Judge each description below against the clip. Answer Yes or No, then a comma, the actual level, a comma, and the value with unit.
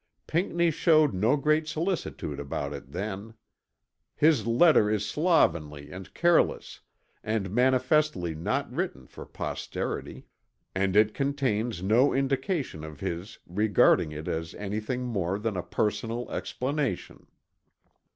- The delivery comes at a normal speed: No, slow, 120 wpm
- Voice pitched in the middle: No, low, 110 Hz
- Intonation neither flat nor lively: No, wide, 7.2 semitones